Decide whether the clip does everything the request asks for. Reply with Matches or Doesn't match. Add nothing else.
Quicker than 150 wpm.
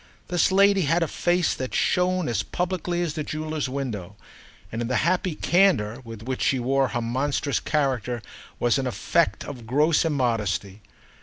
Matches